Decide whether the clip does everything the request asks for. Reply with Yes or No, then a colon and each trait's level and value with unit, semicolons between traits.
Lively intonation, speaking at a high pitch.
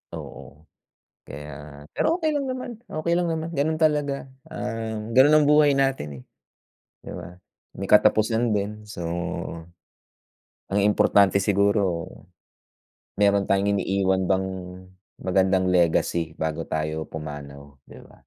No: wide, 8.1 semitones; low, 100 Hz